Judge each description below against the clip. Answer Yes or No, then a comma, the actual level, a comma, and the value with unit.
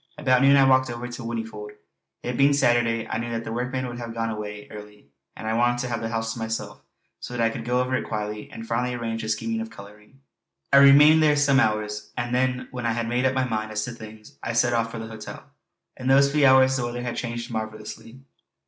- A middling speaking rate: No, fast, 245 wpm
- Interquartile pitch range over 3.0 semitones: No, narrow, 2.4 semitones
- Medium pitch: No, low, 120 Hz